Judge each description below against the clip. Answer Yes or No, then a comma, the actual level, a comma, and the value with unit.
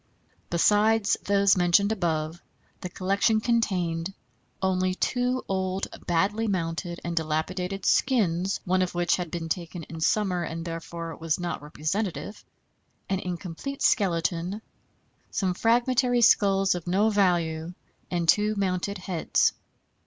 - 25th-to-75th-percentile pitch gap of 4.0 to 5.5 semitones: No, average, 3.1 semitones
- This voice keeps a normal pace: No, slow, 125 wpm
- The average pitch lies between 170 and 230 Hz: Yes, medium, 185 Hz